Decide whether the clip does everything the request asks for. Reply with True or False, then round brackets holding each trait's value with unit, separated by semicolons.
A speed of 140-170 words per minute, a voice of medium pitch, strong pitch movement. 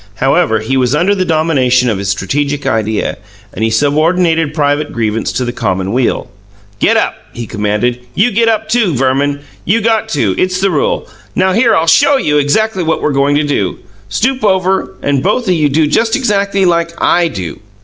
False (190 wpm; 150 Hz; 7.2 semitones)